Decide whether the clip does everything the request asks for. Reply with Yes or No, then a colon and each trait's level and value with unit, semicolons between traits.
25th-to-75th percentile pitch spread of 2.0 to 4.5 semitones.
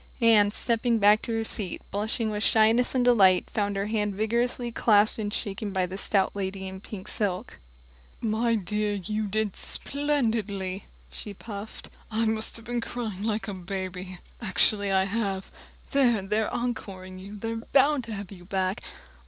Yes: average, 2.7 semitones